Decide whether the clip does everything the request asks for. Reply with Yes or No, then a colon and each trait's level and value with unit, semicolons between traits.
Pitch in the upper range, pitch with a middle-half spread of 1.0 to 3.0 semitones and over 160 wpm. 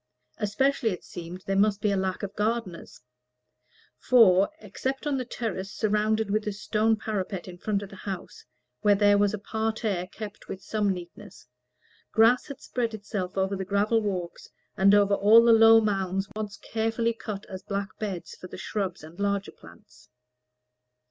Yes: high, 205 Hz; narrow, 2.4 semitones; average, 170 wpm